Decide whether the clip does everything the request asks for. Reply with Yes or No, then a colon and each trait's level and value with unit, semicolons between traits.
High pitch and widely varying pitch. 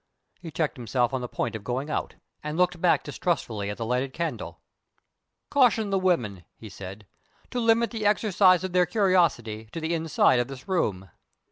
No: medium, 160 Hz; wide, 7.8 semitones